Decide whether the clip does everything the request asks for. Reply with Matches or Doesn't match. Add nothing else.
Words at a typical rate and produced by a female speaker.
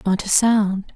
Matches